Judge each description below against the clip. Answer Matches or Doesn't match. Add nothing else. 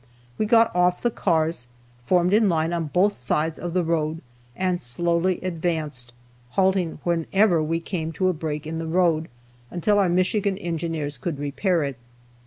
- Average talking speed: Matches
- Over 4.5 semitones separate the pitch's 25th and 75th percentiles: Doesn't match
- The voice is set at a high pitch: Doesn't match